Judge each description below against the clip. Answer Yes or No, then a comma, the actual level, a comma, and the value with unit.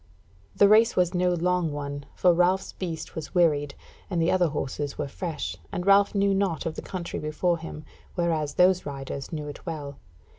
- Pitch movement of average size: Yes, average, 3.5 semitones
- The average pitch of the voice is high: No, medium, 170 Hz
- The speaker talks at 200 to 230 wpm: No, average, 185 wpm